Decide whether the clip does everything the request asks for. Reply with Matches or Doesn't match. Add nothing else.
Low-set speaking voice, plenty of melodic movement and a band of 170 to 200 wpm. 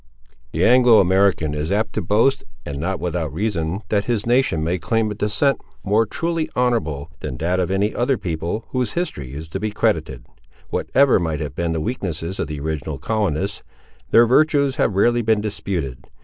Matches